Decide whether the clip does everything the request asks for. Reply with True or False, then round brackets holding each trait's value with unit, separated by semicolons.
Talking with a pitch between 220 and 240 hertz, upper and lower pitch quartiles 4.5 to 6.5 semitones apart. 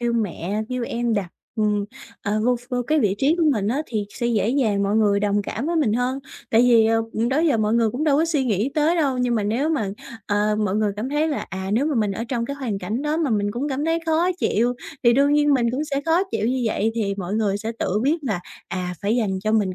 True (235 Hz; 4.9 semitones)